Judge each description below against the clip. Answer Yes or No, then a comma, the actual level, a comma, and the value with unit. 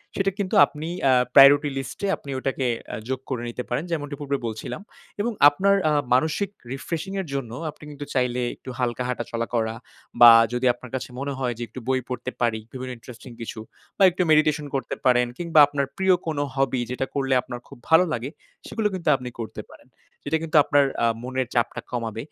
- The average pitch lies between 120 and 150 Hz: Yes, low, 135 Hz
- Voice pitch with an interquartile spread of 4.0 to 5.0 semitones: No, average, 3.5 semitones